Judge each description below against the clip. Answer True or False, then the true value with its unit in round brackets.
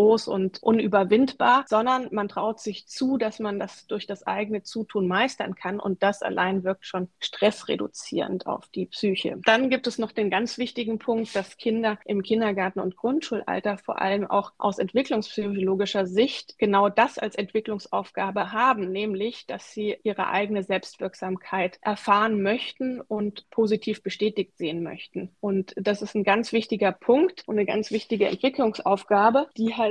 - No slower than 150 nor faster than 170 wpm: True (155 wpm)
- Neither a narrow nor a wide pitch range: False (2.3 semitones)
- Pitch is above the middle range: True (210 Hz)